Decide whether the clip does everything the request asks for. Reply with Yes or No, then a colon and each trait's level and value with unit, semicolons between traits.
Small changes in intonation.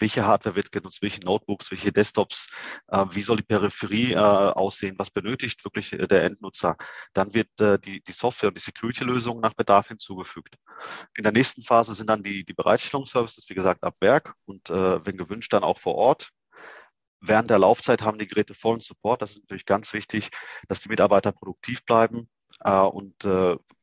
Yes: narrow, 2.3 semitones